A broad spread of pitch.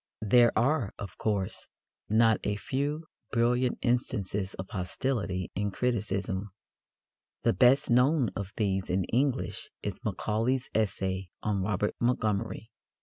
No: average, 4.1 semitones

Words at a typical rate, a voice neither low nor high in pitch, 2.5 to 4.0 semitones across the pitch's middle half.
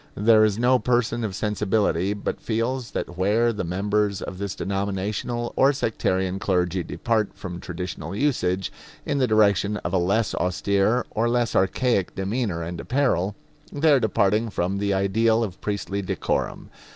No: average, 155 wpm; low, 105 Hz; average, 3.3 semitones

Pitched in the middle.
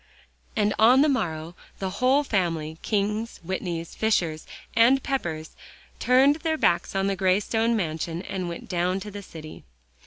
No: high, 195 Hz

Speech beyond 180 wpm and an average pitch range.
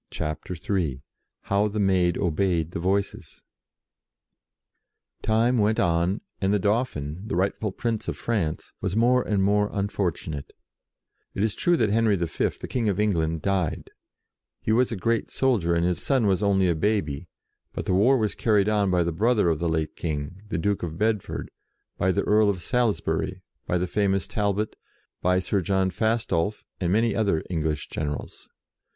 No: average, 170 wpm; average, 3.9 semitones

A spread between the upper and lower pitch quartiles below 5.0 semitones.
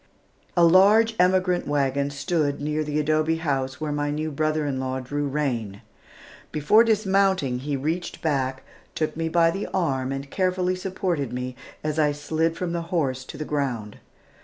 Yes: average, 4.0 semitones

